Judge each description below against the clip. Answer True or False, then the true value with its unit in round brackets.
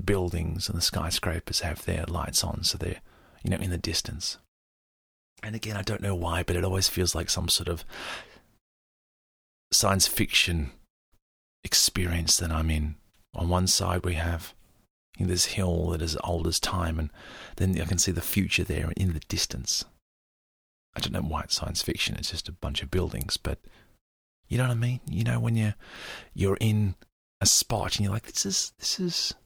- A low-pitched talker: True (90 Hz)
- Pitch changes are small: False (3.3 semitones)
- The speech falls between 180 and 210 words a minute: True (185 wpm)